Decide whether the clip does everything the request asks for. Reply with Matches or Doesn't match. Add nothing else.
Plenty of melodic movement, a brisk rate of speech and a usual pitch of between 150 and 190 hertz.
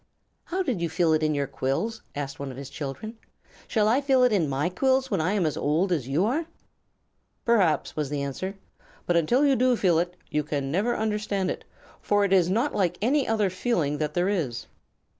Matches